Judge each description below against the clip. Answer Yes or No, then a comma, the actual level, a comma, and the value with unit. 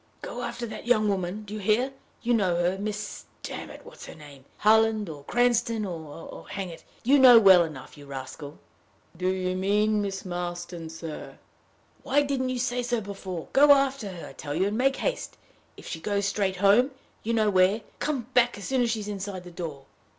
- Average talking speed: No, fast, 215 wpm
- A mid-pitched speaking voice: No, high, 205 Hz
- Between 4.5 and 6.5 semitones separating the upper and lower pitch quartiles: Yes, average, 5.0 semitones